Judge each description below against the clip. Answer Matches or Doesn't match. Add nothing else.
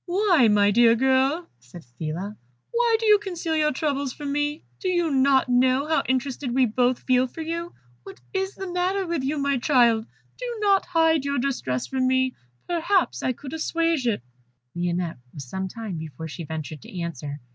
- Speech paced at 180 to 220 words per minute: Matches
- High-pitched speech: Matches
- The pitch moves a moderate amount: Doesn't match